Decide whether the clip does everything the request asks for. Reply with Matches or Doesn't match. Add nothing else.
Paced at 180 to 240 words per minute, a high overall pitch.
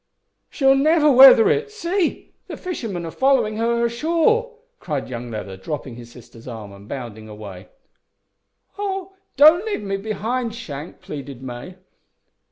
Doesn't match